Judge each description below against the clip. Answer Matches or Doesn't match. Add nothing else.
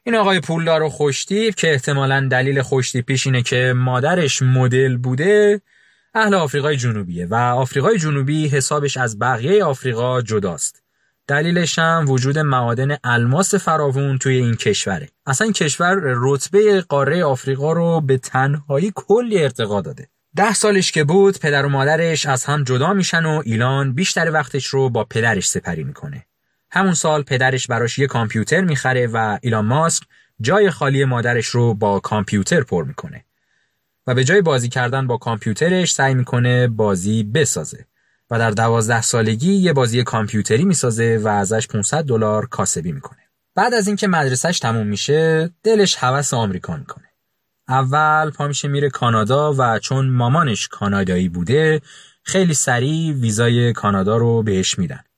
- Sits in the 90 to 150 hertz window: Matches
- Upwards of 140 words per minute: Matches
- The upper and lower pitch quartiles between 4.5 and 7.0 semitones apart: Matches